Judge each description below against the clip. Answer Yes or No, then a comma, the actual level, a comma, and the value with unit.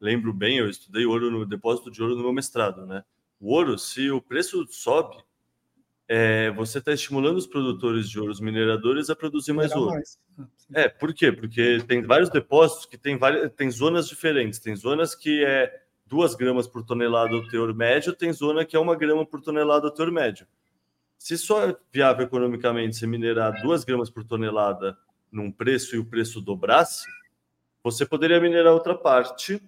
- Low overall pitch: Yes, low, 125 Hz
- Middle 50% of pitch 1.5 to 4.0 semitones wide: No, wide, 5.5 semitones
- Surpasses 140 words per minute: Yes, average, 180 wpm